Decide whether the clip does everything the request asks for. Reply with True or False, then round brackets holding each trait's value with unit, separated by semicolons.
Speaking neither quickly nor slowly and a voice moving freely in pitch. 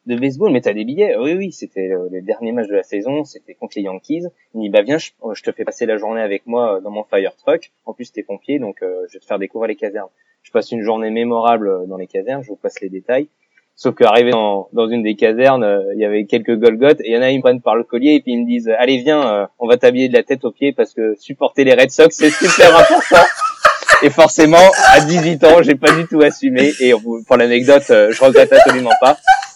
False (260 wpm; 6.3 semitones)